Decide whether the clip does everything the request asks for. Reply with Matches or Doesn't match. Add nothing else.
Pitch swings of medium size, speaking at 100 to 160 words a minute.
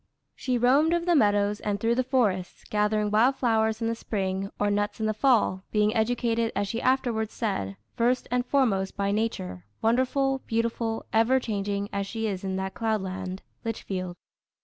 Doesn't match